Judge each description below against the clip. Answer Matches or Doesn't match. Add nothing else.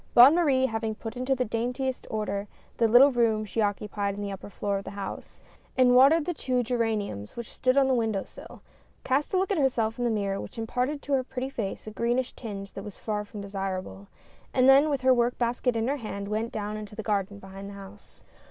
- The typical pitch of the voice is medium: Doesn't match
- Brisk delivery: Matches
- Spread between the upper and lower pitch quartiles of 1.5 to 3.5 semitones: Doesn't match